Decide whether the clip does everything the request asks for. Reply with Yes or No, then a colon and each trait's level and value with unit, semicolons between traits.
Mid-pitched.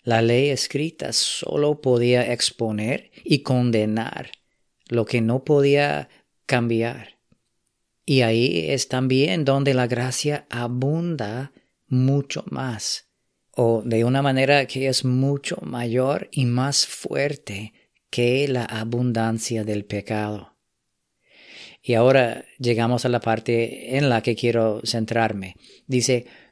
No: low, 125 Hz